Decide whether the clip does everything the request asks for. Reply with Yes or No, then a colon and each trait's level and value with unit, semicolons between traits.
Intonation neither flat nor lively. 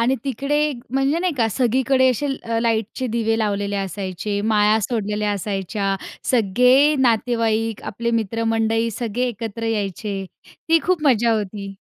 Yes: average, 3.3 semitones